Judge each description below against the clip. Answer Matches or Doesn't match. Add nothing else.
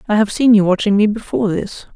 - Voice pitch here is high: Matches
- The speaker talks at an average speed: Doesn't match